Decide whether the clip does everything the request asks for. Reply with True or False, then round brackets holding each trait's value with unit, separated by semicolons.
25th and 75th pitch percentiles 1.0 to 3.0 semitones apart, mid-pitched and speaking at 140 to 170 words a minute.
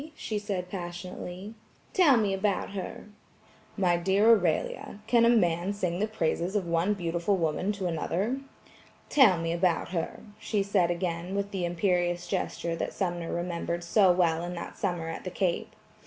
True (2.7 semitones; 180 Hz; 165 wpm)